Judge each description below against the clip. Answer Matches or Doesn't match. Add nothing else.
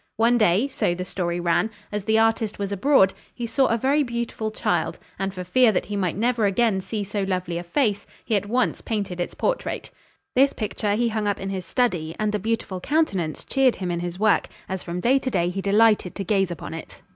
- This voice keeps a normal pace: Doesn't match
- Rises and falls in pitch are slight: Doesn't match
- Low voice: Doesn't match